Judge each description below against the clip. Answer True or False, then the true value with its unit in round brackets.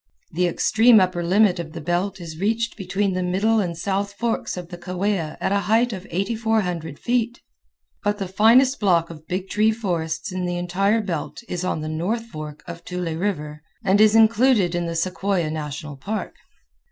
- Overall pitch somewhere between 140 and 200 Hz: True (185 Hz)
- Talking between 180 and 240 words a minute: True (185 wpm)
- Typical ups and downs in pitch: True (3.9 semitones)